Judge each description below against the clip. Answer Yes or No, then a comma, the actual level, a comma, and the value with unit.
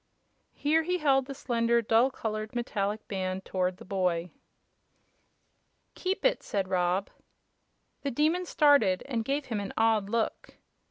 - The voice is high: Yes, high, 225 Hz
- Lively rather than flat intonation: Yes, wide, 6.2 semitones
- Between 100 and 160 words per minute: Yes, average, 140 wpm